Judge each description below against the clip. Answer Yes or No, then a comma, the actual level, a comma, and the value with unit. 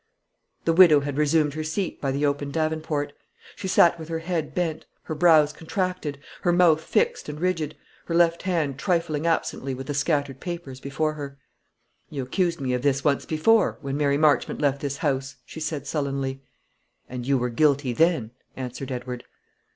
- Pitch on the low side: No, medium, 150 Hz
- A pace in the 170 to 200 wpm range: Yes, average, 175 wpm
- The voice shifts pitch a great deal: No, average, 3.0 semitones